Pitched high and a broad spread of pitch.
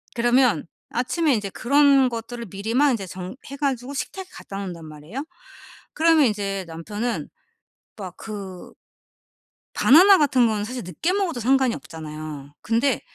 Yes: high, 230 Hz; wide, 6.0 semitones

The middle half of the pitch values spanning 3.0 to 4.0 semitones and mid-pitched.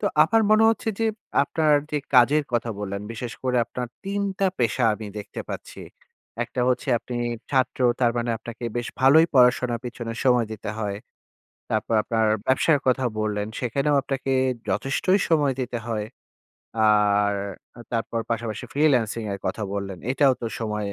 No: average, 3.7 semitones; low, 120 Hz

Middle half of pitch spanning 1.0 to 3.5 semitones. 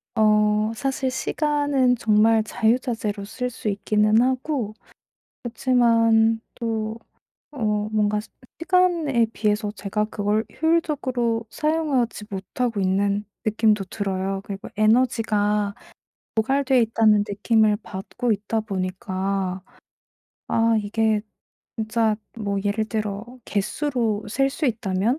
Yes: average, 2.9 semitones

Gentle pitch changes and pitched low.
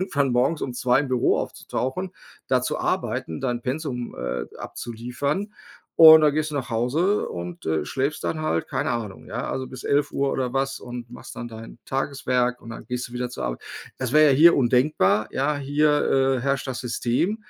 No: average, 3.2 semitones; low, 130 Hz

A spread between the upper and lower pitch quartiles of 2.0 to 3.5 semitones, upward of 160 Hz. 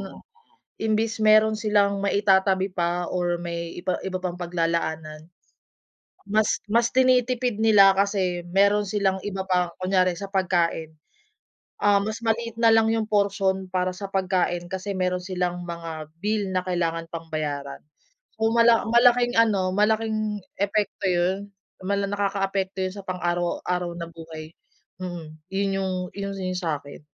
Yes: average, 2.9 semitones; high, 190 Hz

